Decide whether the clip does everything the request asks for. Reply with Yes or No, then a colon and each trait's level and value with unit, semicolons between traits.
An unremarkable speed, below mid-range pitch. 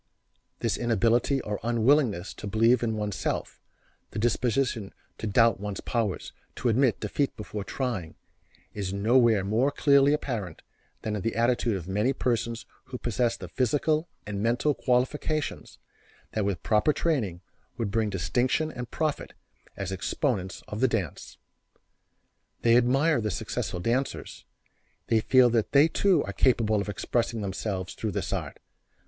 Yes: average, 145 wpm; low, 115 Hz